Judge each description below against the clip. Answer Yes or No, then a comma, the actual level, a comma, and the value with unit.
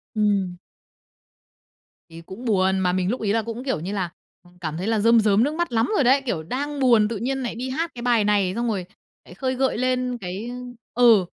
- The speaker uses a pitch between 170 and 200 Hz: No, high, 225 Hz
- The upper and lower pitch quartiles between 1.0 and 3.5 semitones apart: No, average, 4.8 semitones